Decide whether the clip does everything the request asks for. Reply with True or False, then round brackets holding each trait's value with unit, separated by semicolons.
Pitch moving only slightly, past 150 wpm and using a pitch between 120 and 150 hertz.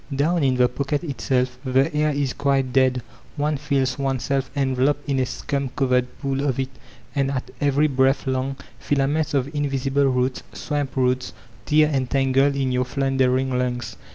True (1.6 semitones; 170 wpm; 135 Hz)